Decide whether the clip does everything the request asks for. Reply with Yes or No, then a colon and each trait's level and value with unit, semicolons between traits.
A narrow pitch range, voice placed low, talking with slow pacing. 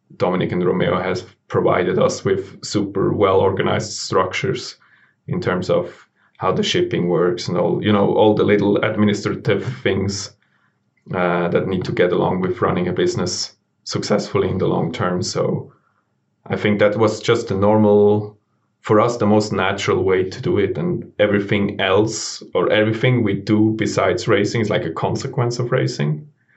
No: narrow, 1.6 semitones; low, 105 Hz; average, 165 wpm